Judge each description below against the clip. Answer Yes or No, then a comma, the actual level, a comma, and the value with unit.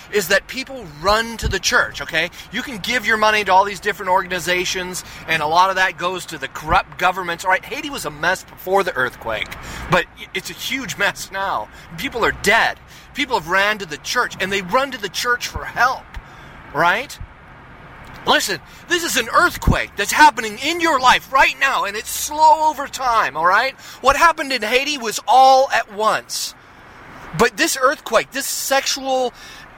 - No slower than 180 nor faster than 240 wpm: Yes, average, 185 wpm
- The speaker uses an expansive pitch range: Yes, wide, 6.0 semitones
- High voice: Yes, high, 215 Hz